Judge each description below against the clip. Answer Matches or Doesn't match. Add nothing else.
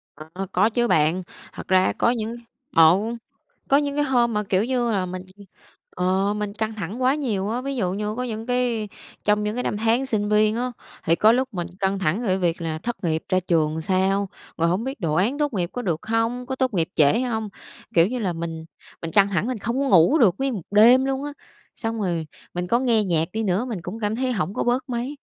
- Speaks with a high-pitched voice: Matches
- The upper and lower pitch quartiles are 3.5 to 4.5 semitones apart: Doesn't match